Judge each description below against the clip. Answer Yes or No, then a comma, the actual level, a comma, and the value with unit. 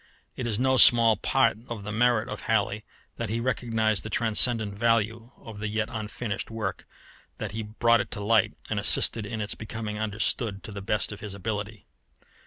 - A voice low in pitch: Yes, low, 110 Hz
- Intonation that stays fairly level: Yes, narrow, 1.8 semitones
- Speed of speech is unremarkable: Yes, average, 190 wpm